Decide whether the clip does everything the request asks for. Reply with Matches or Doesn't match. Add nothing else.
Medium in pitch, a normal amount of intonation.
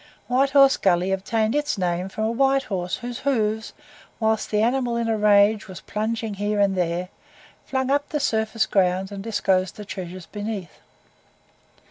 Doesn't match